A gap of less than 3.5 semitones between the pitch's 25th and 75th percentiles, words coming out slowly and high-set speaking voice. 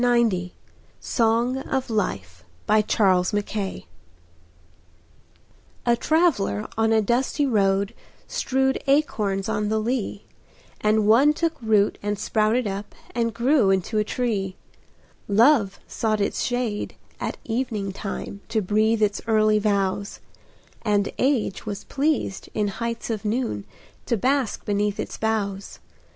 Yes: average, 3.0 semitones; slow, 120 wpm; high, 215 Hz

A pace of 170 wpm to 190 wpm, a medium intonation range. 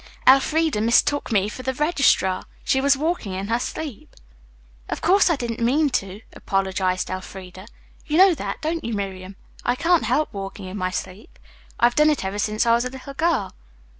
No: average, 185 wpm; wide, 7.5 semitones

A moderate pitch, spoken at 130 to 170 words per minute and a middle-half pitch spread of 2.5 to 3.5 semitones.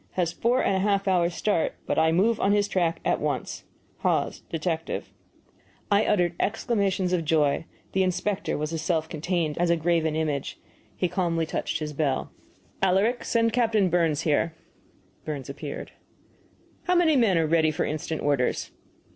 No: medium, 170 Hz; average, 165 wpm; average, 3.9 semitones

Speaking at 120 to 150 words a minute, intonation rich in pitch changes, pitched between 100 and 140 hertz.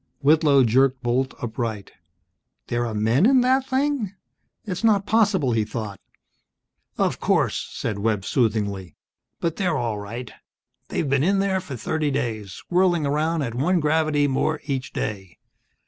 Yes: average, 145 wpm; wide, 7.7 semitones; low, 135 Hz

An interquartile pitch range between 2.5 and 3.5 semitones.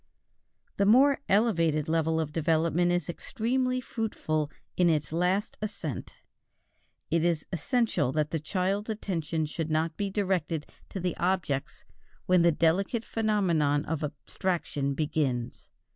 No: average, 4.3 semitones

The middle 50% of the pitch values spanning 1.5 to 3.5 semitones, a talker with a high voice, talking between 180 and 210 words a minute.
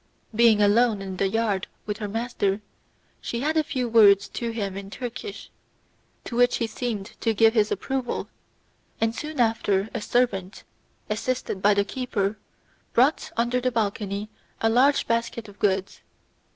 No: average, 3.2 semitones; high, 225 Hz; average, 155 wpm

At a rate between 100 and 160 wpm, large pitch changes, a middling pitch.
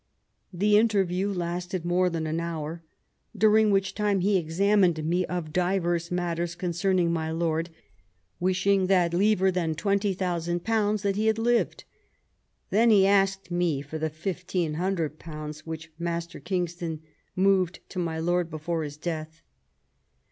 No: average, 145 wpm; average, 2.8 semitones; medium, 175 Hz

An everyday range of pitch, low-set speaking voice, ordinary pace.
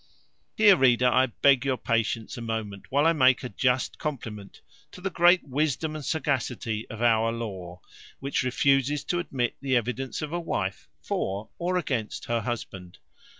Yes: average, 4.3 semitones; low, 125 Hz; average, 165 wpm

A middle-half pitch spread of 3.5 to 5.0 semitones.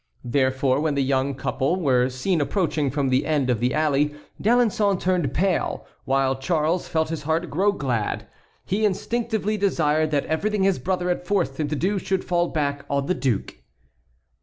No: wide, 5.4 semitones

